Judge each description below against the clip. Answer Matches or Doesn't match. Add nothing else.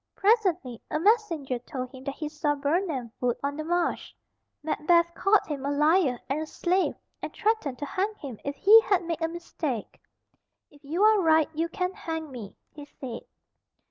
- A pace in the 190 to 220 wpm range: Doesn't match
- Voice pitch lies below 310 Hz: Doesn't match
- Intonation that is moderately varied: Matches